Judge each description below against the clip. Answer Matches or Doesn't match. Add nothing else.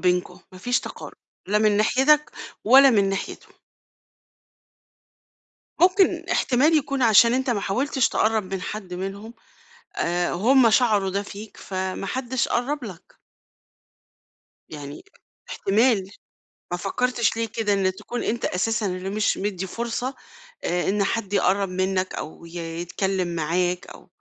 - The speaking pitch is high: Matches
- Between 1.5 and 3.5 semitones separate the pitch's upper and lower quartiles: Doesn't match